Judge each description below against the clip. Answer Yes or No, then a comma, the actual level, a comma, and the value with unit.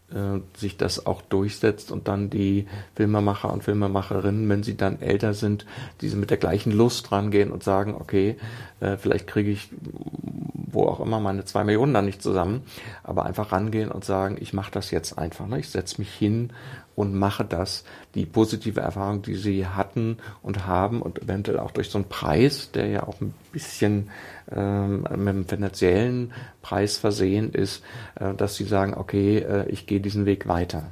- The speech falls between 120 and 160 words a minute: No, average, 180 wpm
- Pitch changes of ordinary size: No, narrow, 1.7 semitones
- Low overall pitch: Yes, low, 100 Hz